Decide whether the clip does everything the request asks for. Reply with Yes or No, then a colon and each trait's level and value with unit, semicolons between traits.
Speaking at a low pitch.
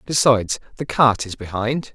Yes: low, 120 Hz